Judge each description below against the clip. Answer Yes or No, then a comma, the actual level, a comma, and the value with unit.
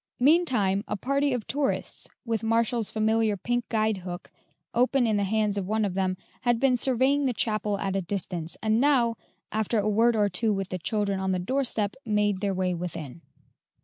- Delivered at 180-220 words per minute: Yes, average, 190 wpm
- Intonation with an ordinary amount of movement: Yes, average, 3.6 semitones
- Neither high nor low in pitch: No, high, 215 Hz